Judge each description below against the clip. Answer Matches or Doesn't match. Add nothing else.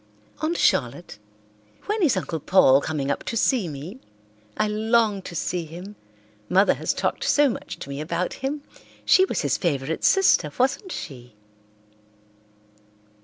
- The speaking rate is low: Doesn't match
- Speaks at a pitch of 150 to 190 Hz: Matches